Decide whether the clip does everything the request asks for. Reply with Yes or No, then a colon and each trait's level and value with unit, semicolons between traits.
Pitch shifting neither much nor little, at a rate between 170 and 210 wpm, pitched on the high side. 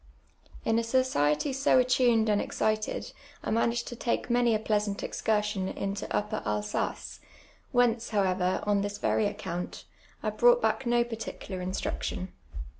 No: average, 3.3 semitones; average, 140 wpm; high, 215 Hz